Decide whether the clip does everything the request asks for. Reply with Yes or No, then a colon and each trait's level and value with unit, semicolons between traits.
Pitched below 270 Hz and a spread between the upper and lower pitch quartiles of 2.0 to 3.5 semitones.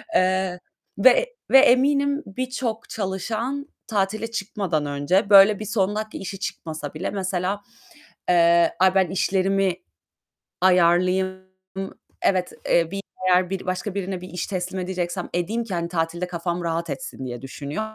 Yes: medium, 185 Hz; average, 2.9 semitones